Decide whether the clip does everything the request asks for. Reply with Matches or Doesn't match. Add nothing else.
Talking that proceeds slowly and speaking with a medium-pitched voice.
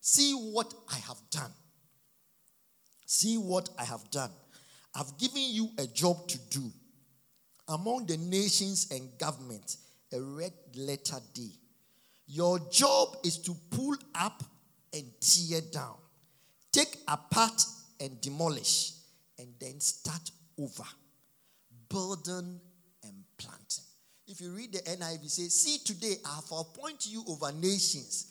Matches